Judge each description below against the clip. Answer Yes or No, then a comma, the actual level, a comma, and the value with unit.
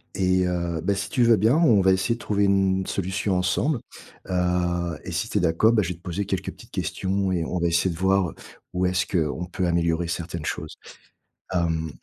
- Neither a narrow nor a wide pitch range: No, narrow, 2.3 semitones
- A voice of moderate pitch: No, very low, 90 Hz